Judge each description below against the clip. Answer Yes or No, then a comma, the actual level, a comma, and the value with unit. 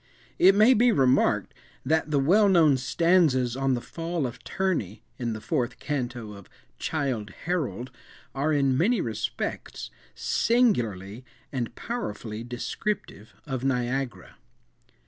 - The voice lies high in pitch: No, low, 135 Hz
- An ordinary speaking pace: No, slow, 125 wpm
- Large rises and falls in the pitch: Yes, wide, 6.0 semitones